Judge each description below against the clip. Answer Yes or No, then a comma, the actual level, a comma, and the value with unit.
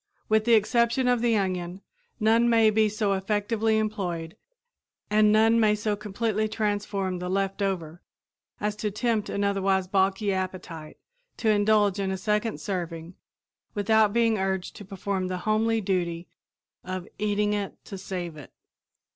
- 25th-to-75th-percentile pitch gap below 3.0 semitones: Yes, narrow, 2.4 semitones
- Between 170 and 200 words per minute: No, average, 150 wpm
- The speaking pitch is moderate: No, high, 205 Hz